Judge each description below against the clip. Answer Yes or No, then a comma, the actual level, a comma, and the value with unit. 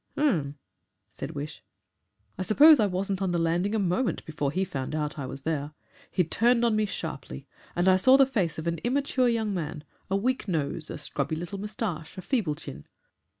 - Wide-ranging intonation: Yes, wide, 6.1 semitones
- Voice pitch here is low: No, medium, 185 Hz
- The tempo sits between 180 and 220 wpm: Yes, average, 195 wpm